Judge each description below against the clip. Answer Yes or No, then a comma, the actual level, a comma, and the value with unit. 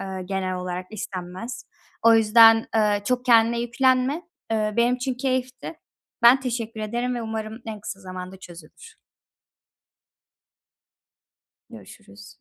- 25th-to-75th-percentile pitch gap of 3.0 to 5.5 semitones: Yes, average, 4.3 semitones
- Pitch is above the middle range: Yes, high, 225 Hz